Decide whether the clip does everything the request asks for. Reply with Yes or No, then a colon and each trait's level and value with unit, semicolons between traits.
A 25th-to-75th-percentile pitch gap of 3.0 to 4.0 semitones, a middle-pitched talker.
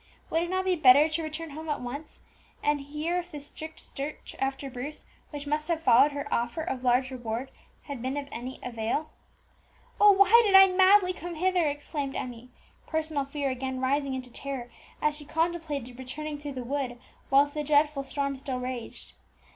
No: average, 3.3 semitones; very high, 285 Hz